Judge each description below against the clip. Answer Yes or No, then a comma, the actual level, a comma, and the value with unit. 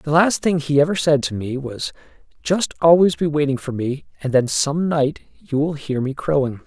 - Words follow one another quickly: Yes, fast, 215 wpm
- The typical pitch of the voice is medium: Yes, medium, 145 Hz